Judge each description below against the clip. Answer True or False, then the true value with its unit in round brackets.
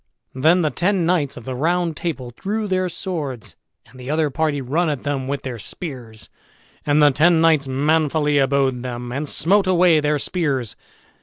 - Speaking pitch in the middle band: True (150 Hz)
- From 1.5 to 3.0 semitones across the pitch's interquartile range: False (4.2 semitones)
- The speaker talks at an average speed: True (175 wpm)